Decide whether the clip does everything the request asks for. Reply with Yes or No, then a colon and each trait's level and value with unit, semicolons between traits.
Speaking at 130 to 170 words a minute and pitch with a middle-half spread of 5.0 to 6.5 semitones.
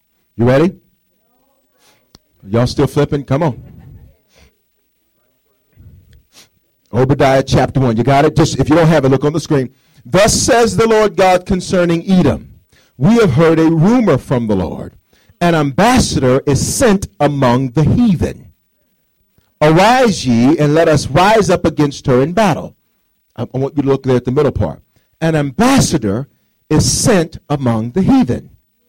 Yes: average, 150 wpm; wide, 5.5 semitones